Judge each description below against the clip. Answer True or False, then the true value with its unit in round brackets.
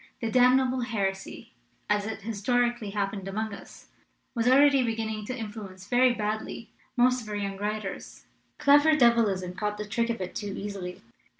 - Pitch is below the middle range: False (220 Hz)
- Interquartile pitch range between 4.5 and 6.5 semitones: False (3.3 semitones)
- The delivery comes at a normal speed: True (170 wpm)